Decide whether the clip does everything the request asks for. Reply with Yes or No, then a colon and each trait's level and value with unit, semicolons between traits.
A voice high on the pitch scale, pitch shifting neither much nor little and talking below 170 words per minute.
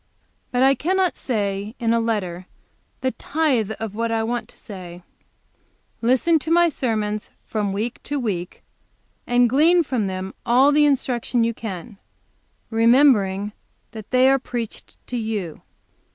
Yes: high, 230 Hz; average, 4.0 semitones; average, 145 wpm